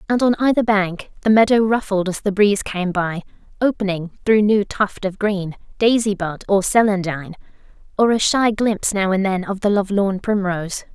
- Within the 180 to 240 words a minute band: Yes, average, 185 wpm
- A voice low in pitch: No, high, 200 Hz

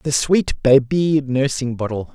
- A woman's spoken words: No, male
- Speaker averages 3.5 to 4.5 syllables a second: Yes, 3.9 syllables/s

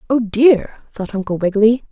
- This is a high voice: Yes, high, 220 Hz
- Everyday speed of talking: Yes, average, 155 wpm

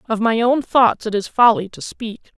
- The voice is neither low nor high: No, high, 230 Hz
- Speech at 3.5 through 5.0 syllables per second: Yes, 4.7 syllables/s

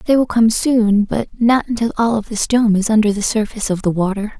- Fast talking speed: Yes, fast, 245 wpm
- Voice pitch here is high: Yes, high, 220 Hz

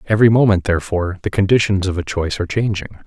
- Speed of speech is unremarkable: Yes, average, 195 wpm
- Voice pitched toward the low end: Yes, very low, 95 Hz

